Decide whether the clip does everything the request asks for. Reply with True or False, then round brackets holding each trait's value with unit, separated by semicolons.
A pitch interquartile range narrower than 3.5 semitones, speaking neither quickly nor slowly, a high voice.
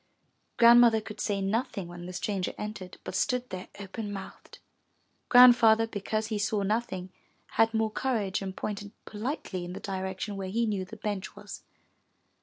True (2.9 semitones; 160 wpm; 210 Hz)